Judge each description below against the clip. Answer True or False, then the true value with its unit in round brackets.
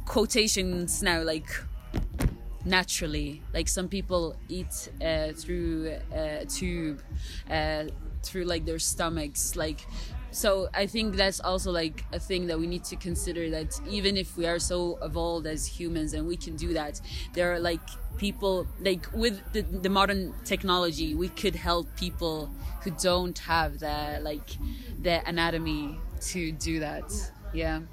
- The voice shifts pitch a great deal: False (2.7 semitones)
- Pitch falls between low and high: True (170 Hz)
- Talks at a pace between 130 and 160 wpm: True (150 wpm)